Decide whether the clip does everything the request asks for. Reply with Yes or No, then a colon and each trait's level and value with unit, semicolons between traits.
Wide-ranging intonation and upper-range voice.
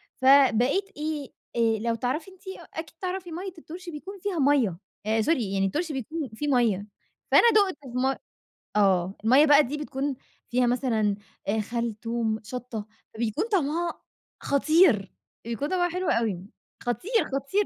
Yes: wide, 6.6 semitones; very high, 270 Hz